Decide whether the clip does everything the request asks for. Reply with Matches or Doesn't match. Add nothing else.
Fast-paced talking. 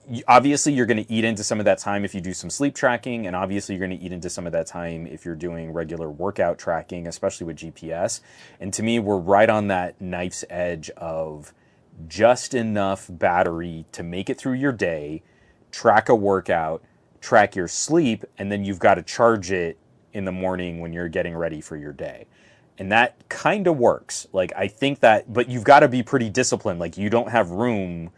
Matches